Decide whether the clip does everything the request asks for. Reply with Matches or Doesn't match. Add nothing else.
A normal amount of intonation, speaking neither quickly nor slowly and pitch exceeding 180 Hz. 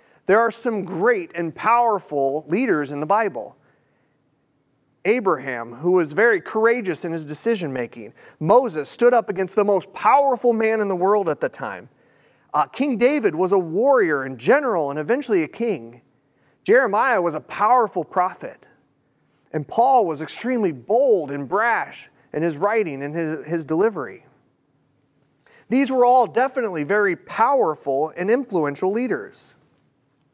Doesn't match